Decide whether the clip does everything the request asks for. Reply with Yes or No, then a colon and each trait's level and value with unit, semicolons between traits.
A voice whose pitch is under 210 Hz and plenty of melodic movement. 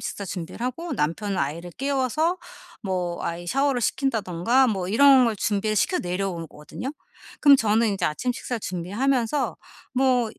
No: high, 220 Hz; wide, 6.5 semitones